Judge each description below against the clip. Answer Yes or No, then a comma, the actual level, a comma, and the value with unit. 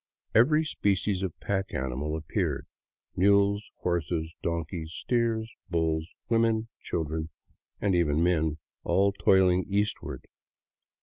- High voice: No, very low, 90 Hz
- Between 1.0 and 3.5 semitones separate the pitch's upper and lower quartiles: No, average, 4.1 semitones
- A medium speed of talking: No, slow, 110 wpm